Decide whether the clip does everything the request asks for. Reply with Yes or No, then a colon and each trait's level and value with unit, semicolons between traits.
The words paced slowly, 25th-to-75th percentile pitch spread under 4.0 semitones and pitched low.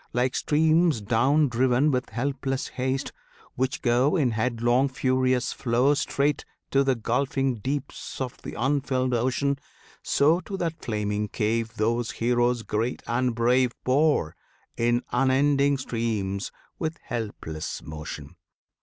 Yes: slow, 125 wpm; average, 3.0 semitones; low, 125 Hz